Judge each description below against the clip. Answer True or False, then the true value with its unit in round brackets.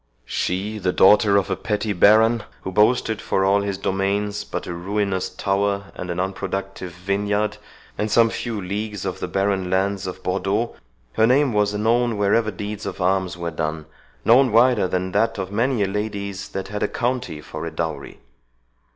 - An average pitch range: False (2.2 semitones)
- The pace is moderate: True (175 wpm)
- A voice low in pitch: True (100 Hz)